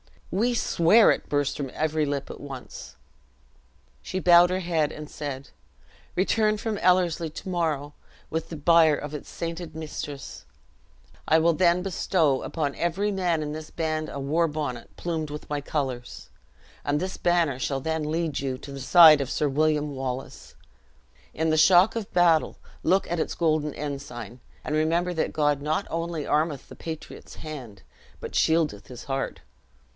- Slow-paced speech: No, average, 165 wpm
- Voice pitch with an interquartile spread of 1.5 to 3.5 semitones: Yes, average, 2.9 semitones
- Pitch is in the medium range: Yes, medium, 155 Hz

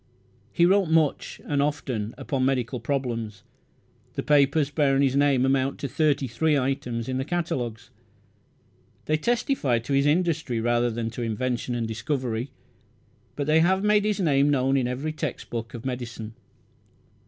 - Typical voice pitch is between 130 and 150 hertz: Yes, low, 135 Hz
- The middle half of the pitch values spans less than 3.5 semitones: No, average, 3.8 semitones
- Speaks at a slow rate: No, average, 155 wpm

